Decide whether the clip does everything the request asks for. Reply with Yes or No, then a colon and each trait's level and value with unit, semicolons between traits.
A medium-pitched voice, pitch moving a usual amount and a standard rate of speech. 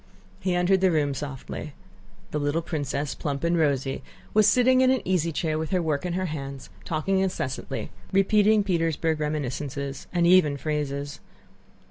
Yes: medium, 155 Hz; average, 4.4 semitones; average, 155 wpm